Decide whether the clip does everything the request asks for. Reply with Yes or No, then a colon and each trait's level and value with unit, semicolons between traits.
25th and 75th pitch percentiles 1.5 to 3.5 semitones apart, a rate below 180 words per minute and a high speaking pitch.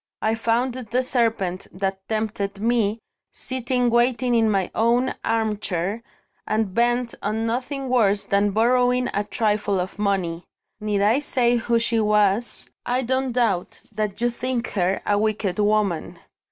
Yes: average, 3.1 semitones; average, 145 wpm; high, 220 Hz